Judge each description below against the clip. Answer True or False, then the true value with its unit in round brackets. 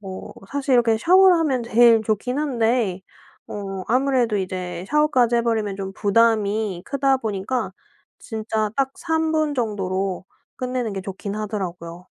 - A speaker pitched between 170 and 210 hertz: False (225 Hz)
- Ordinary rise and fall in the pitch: True (4.7 semitones)